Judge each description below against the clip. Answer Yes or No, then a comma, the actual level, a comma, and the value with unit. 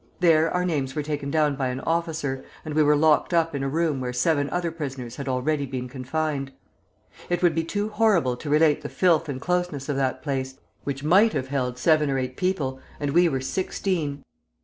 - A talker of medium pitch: Yes, medium, 150 Hz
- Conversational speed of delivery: No, fast, 210 wpm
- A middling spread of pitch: Yes, average, 3.6 semitones